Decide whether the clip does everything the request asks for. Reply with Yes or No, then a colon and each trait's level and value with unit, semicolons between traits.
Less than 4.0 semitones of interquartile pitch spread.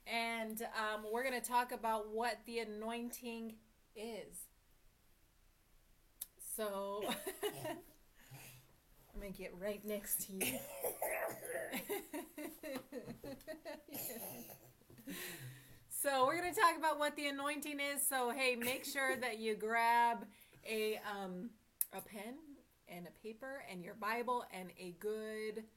No: average, 4.3 semitones